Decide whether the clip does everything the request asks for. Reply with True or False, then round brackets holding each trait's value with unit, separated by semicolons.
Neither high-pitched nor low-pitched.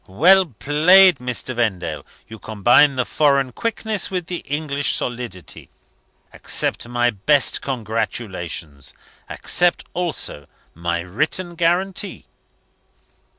False (130 Hz)